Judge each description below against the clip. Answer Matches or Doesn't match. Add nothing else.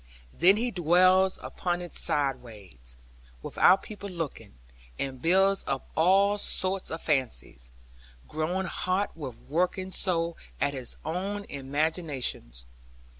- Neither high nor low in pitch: Matches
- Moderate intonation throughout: Doesn't match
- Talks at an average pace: Doesn't match